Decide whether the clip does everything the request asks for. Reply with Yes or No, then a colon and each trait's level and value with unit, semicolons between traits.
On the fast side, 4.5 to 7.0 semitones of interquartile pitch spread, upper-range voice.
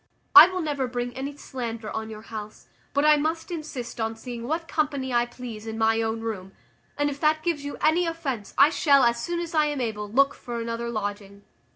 Yes: fast, 215 wpm; average, 5.2 semitones; very high, 250 Hz